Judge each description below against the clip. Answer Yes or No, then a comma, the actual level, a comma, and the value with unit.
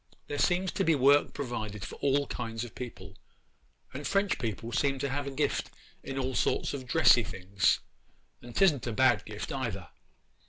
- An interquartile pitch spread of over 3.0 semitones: Yes, average, 3.8 semitones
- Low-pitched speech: Yes, low, 130 Hz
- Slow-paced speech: No, average, 175 wpm